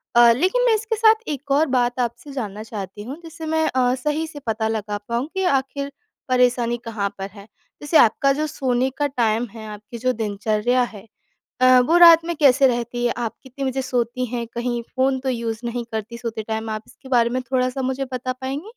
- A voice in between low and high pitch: No, very high, 250 Hz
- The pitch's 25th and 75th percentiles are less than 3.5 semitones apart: Yes, average, 3.1 semitones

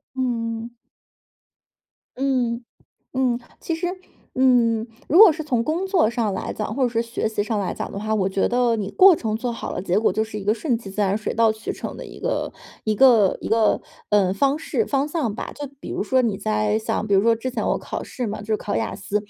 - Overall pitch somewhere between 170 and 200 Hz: No, high, 230 Hz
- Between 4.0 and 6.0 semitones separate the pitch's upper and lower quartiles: No, average, 3.4 semitones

